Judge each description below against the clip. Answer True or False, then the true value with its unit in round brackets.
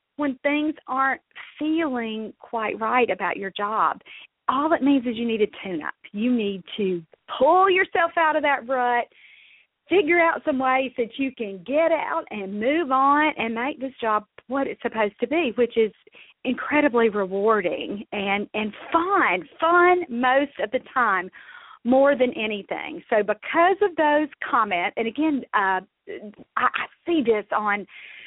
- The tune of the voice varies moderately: False (6.3 semitones)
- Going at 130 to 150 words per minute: False (160 wpm)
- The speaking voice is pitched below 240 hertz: False (260 Hz)